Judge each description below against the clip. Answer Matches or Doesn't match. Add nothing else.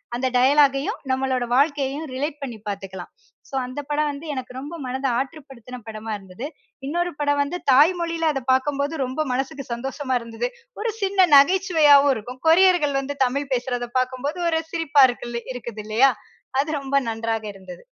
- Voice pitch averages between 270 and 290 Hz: Matches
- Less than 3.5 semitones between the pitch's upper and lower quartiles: Matches